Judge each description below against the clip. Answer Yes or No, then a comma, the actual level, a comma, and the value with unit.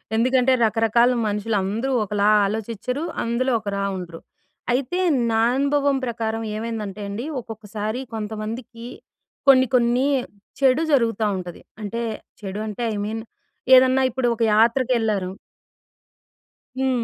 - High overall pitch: Yes, high, 230 Hz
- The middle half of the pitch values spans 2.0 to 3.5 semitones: Yes, average, 3.2 semitones